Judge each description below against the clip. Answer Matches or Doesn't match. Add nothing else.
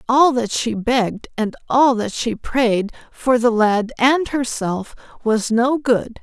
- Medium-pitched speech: Doesn't match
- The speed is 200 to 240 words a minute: Doesn't match